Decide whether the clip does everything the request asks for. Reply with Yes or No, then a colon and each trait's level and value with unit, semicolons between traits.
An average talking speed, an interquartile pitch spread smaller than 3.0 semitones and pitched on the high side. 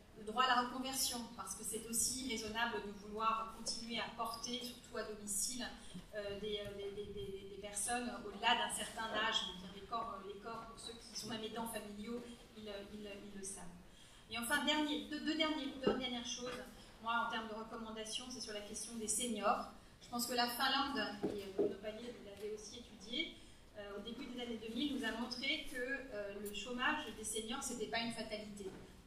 Yes: average, 200 wpm; narrow, 2.5 semitones; high, 225 Hz